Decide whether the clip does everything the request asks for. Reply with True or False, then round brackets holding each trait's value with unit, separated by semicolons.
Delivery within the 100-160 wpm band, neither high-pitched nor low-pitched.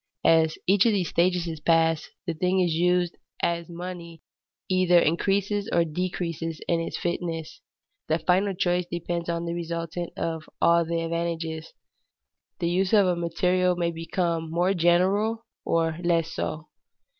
True (145 wpm; 170 Hz)